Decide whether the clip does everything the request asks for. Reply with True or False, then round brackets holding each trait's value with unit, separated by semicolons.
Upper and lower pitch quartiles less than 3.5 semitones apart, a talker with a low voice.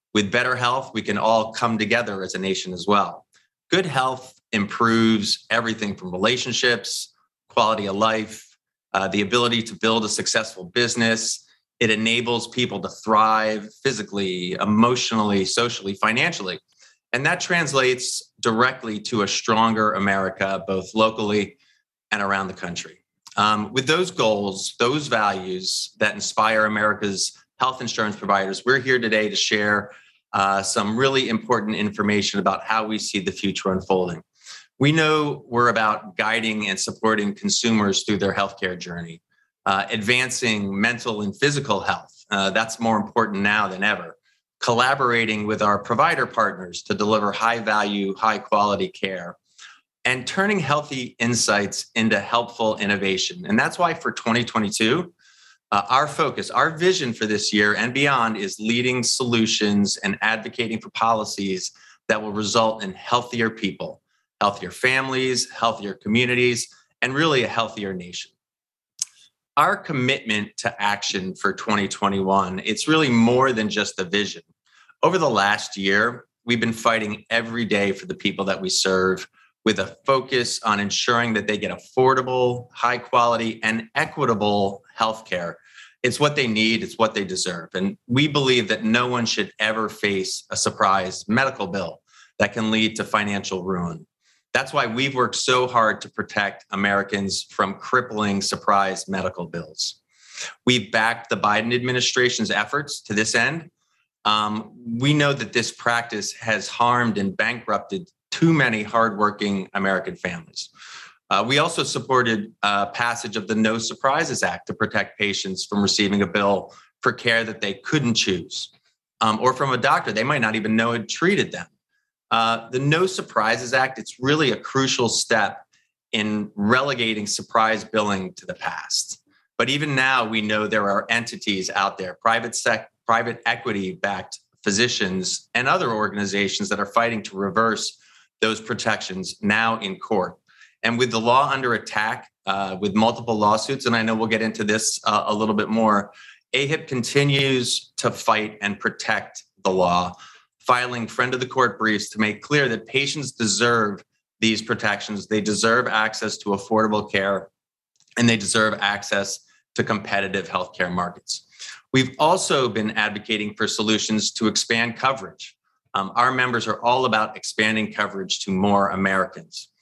True (3.0 semitones; 110 Hz)